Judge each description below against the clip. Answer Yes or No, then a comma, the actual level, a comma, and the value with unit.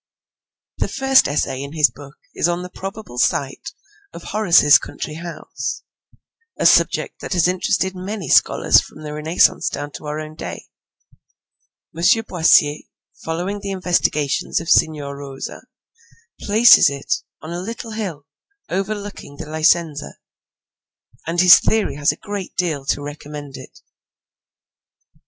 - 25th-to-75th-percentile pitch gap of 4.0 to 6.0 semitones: Yes, average, 4.7 semitones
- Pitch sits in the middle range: Yes, medium, 165 Hz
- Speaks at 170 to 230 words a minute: No, average, 140 wpm